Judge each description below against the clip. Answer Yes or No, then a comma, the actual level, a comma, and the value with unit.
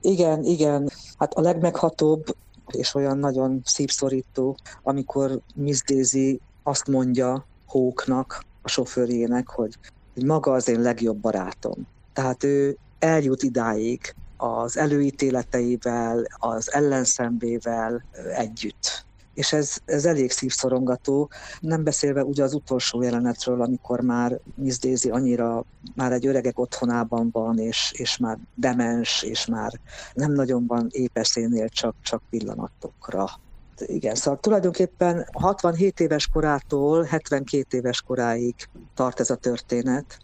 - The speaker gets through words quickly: No, average, 120 wpm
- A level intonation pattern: No, average, 3.0 semitones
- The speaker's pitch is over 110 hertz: Yes, low, 130 Hz